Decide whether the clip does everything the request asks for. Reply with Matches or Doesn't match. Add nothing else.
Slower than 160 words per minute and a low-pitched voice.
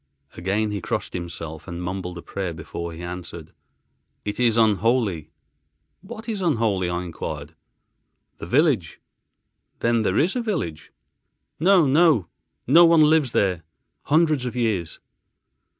Matches